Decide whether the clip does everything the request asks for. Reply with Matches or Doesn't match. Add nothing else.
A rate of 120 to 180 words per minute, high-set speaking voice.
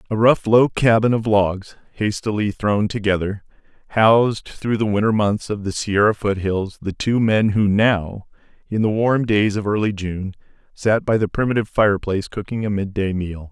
Doesn't match